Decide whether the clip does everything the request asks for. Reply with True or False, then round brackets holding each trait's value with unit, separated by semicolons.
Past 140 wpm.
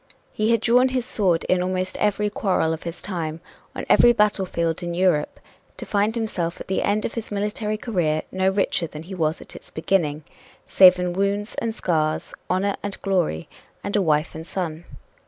True (190 wpm)